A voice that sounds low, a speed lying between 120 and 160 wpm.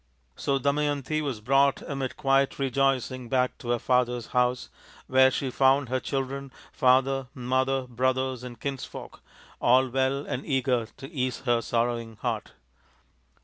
Yes: low, 130 Hz; average, 140 wpm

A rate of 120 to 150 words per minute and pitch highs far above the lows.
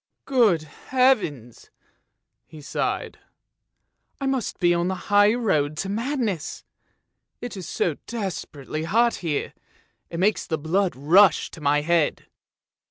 Yes: average, 140 wpm; wide, 6.2 semitones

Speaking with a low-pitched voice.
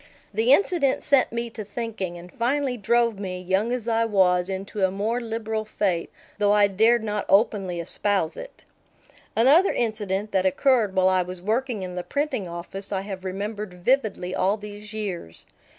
No: high, 210 Hz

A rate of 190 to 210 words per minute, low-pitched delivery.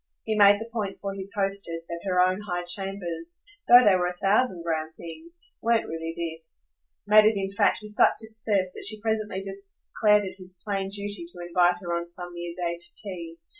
No: fast, 205 wpm; high, 190 Hz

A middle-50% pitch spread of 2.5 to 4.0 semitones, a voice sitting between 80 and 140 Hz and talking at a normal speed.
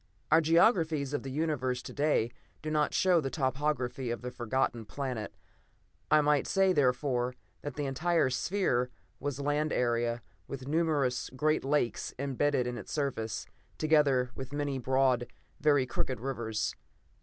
Yes: average, 3.2 semitones; low, 135 Hz; average, 145 wpm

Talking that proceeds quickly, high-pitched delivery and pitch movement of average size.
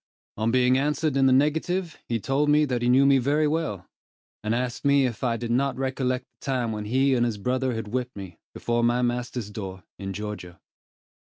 No: fast, 210 wpm; low, 125 Hz; average, 3.2 semitones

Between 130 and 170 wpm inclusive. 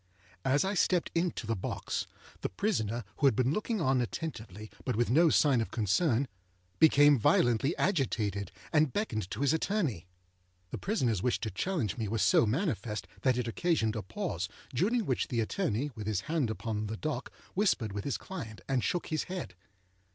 No: average, 180 wpm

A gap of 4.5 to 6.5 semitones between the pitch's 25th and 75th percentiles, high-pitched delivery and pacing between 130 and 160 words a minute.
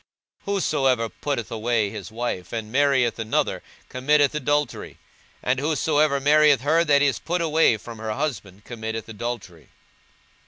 No: average, 4.8 semitones; low, 130 Hz; average, 140 wpm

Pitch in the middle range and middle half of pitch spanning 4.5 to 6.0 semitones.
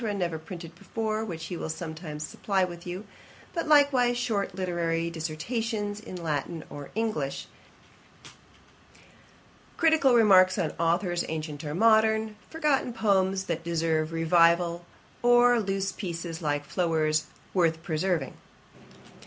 Yes: medium, 180 Hz; average, 5.0 semitones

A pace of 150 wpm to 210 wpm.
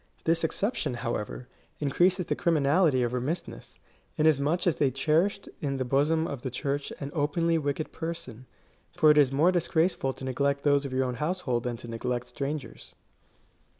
Yes: average, 165 wpm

